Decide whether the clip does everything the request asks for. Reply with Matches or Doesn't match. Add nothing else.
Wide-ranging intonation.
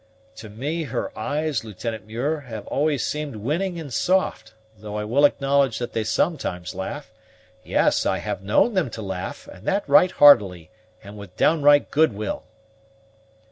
Matches